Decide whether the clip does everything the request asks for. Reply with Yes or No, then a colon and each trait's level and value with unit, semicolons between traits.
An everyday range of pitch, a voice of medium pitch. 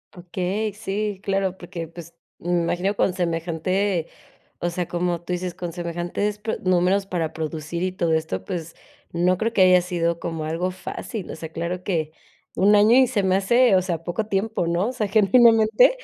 Yes: average, 3.0 semitones; medium, 180 Hz